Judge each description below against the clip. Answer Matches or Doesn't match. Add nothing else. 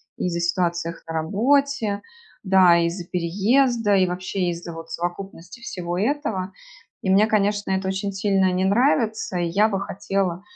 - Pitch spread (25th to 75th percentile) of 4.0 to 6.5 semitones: Doesn't match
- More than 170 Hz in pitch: Matches